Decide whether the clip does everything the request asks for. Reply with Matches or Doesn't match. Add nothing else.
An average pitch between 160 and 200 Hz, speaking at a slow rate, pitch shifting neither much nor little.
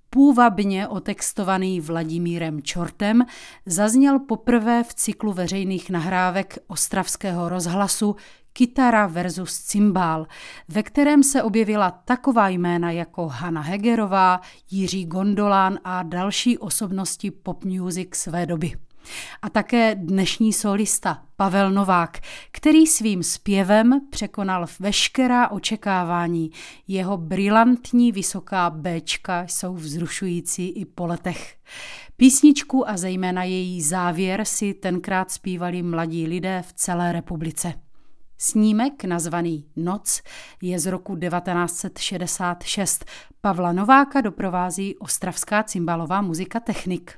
Matches